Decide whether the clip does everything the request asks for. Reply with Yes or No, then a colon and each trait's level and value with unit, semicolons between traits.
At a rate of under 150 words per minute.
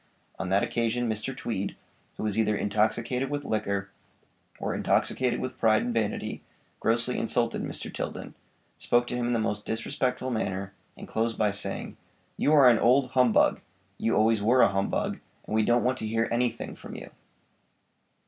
No: average, 170 wpm